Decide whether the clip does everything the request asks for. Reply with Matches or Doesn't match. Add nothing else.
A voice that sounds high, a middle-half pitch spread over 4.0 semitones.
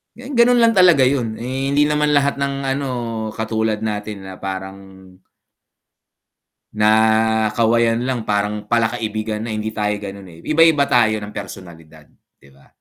Doesn't match